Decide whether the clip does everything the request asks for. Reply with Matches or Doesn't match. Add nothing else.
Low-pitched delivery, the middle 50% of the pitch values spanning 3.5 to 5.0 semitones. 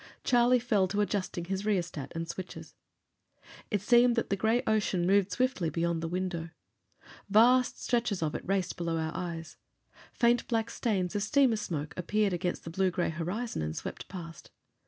Doesn't match